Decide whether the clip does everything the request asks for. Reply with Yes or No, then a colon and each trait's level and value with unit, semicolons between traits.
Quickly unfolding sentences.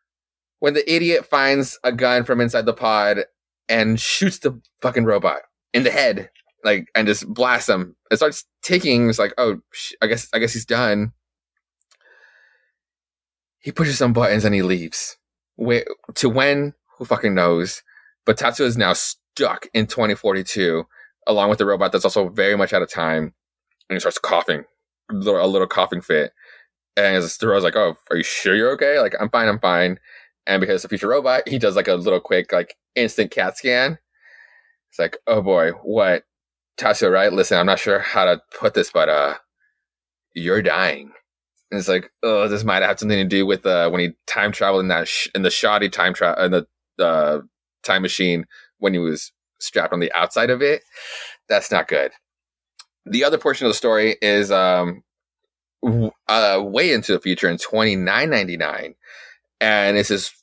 No: average, 185 wpm